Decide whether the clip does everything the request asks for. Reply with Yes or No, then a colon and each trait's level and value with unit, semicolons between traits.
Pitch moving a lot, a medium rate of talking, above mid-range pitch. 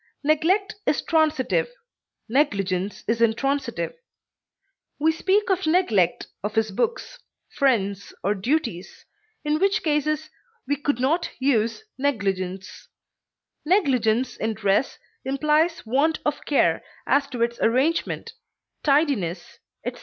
No: wide, 6.1 semitones; slow, 110 wpm; very high, 275 Hz